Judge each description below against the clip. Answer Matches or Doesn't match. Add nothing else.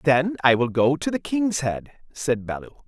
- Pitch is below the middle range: Doesn't match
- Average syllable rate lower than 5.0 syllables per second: Matches